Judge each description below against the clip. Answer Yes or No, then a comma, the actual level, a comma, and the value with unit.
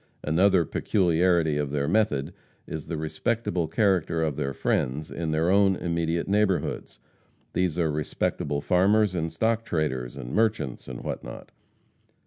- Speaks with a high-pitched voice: No, very low, 85 Hz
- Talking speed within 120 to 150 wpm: Yes, average, 140 wpm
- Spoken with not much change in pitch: No, average, 4.0 semitones